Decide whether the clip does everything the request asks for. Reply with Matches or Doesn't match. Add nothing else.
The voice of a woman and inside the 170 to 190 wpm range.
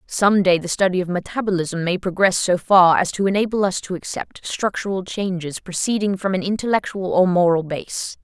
Matches